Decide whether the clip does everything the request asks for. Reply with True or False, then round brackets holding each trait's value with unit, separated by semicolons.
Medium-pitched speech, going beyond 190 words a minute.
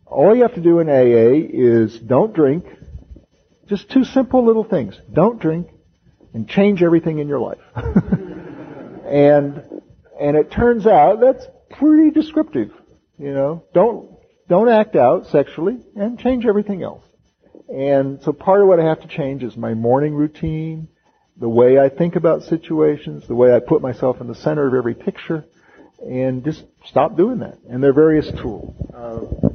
False (155 Hz; 165 wpm)